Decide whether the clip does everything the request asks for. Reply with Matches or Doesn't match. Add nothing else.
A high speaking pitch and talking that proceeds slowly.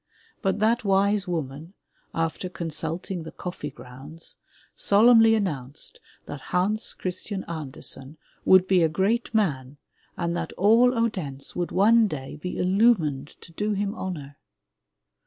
Doesn't match